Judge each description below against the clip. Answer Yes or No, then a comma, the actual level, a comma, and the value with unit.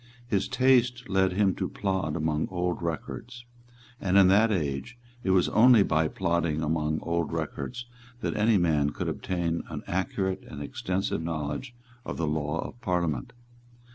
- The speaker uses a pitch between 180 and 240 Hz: No, very low, 90 Hz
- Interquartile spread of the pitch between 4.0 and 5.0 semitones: Yes, average, 4.6 semitones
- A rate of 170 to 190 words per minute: No, average, 155 wpm